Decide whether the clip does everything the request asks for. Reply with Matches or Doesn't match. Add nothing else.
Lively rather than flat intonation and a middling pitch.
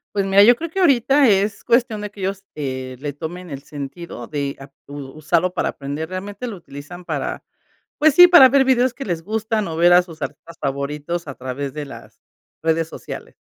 Matches